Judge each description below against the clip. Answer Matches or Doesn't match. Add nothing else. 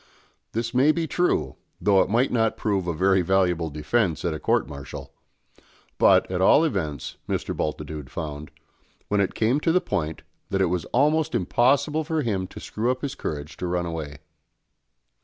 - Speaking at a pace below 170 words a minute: Doesn't match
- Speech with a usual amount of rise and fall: Doesn't match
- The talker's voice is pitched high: Doesn't match